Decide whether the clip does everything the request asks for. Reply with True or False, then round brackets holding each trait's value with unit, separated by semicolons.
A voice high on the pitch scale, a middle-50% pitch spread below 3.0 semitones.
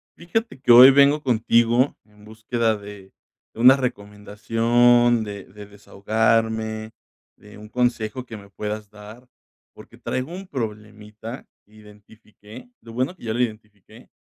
False (110 Hz; 2.6 semitones)